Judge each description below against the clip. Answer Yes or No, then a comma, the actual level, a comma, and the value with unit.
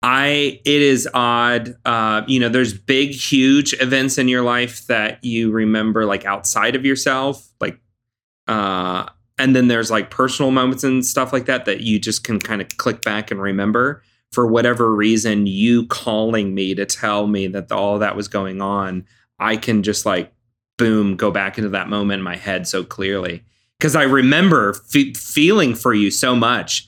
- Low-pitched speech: Yes, low, 115 Hz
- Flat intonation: No, average, 3.8 semitones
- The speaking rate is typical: Yes, average, 185 wpm